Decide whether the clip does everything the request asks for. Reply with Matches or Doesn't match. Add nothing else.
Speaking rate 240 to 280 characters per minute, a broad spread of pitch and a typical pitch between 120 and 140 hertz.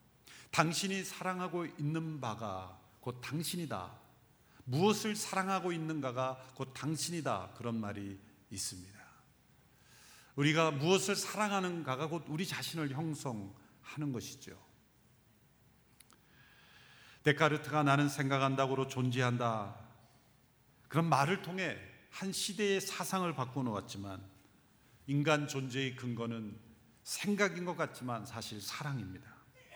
Matches